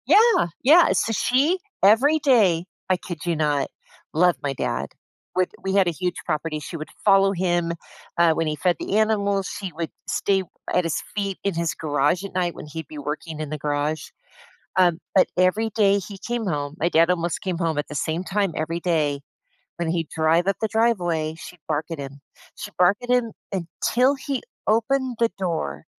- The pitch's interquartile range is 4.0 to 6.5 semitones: Yes, average, 4.3 semitones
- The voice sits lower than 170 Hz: No, medium, 175 Hz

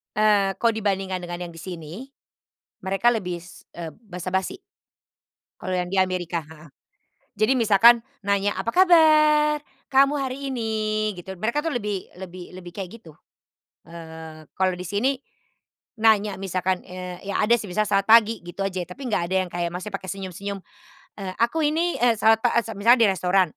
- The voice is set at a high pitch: Yes, high, 195 Hz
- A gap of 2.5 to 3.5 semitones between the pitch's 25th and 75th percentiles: No, average, 4.0 semitones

